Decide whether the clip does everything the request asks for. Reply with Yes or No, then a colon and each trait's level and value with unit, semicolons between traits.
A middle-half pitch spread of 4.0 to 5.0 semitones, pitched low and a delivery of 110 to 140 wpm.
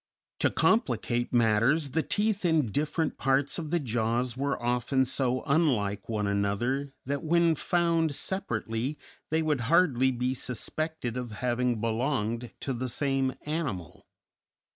Yes: average, 4.6 semitones; low, 130 Hz; slow, 135 wpm